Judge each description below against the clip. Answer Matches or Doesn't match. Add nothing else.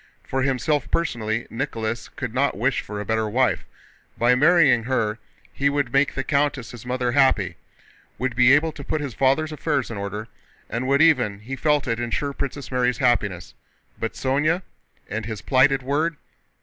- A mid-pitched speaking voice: Doesn't match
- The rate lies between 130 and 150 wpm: Doesn't match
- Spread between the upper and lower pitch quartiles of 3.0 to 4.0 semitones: Matches